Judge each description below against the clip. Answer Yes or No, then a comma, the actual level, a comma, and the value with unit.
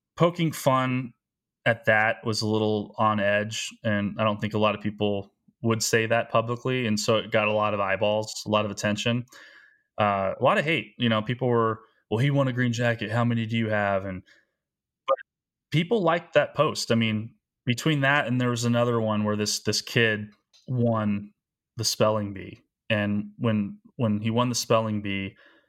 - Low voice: Yes, low, 110 Hz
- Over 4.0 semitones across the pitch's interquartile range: No, narrow, 2.5 semitones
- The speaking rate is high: No, average, 195 wpm